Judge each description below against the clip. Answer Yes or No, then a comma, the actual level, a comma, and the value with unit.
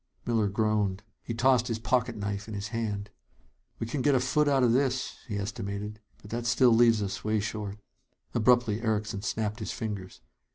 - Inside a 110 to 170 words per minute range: No, average, 180 wpm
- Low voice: Yes, low, 110 Hz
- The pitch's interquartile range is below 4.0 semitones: Yes, average, 2.7 semitones